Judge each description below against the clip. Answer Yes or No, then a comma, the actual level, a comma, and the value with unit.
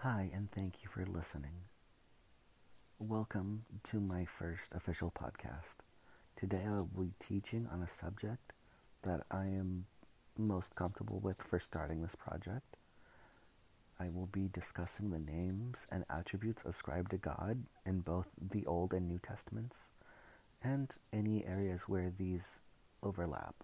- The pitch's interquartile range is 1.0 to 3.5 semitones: Yes, average, 3.0 semitones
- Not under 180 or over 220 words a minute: No, slow, 135 wpm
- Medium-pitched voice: No, very low, 95 Hz